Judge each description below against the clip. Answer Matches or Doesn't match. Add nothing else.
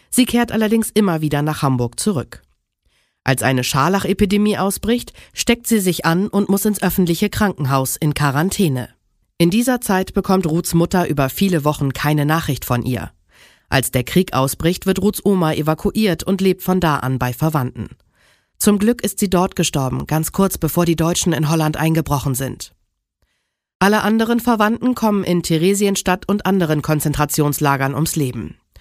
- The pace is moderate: Matches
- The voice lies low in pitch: Doesn't match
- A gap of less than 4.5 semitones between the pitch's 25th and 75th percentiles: Doesn't match